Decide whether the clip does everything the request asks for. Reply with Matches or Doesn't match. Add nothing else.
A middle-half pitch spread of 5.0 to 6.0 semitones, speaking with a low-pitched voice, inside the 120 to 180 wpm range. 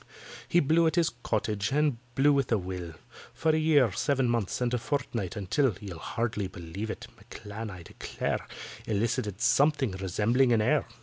Matches